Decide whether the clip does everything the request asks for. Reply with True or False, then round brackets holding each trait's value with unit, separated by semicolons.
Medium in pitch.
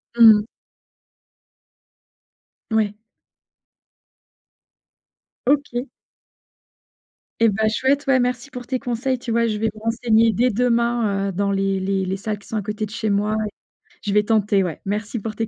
False (220 Hz)